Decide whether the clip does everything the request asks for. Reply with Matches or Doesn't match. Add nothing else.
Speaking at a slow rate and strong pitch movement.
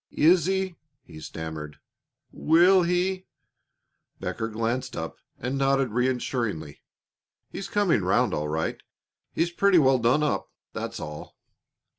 Matches